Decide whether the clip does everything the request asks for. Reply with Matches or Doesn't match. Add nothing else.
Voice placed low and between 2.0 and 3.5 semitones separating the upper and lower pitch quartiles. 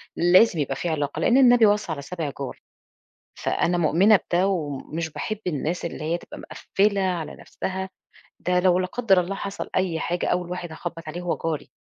Doesn't match